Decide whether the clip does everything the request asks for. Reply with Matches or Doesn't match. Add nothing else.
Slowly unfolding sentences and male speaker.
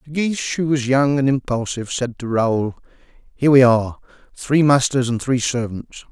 Doesn't match